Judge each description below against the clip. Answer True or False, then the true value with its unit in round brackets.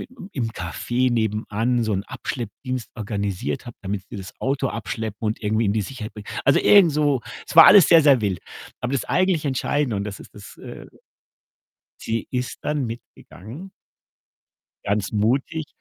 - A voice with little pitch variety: False (4.7 semitones)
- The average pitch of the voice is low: True (115 Hz)